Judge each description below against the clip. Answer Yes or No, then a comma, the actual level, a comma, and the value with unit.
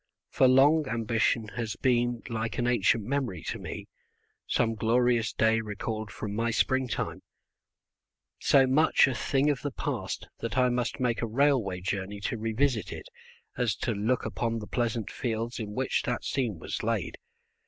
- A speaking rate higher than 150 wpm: Yes, average, 165 wpm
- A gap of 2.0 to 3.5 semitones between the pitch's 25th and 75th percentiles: Yes, narrow, 2.6 semitones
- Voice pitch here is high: No, low, 115 Hz